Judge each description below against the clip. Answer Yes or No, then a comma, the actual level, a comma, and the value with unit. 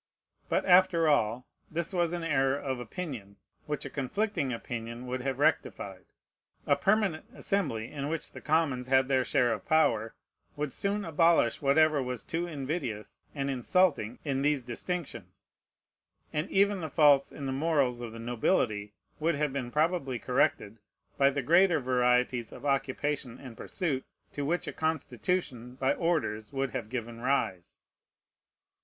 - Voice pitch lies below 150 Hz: Yes, medium, 140 Hz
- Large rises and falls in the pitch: No, average, 4.5 semitones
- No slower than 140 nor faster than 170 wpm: Yes, average, 150 wpm